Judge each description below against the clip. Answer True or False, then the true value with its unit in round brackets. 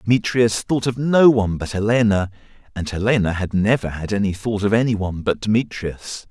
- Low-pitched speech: True (105 Hz)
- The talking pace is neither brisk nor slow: True (170 wpm)